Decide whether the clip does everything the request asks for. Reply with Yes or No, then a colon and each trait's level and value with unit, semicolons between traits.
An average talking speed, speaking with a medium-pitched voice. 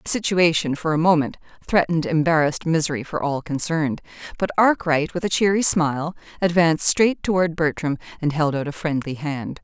Yes: average, 170 wpm; medium, 160 Hz